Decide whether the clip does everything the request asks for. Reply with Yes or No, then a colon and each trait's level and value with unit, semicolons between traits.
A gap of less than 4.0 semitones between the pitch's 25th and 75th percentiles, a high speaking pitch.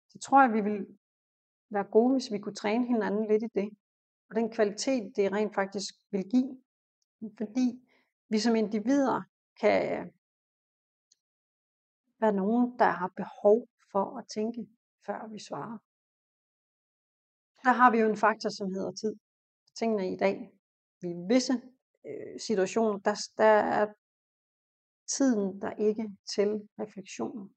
Yes: average, 2.7 semitones; high, 215 Hz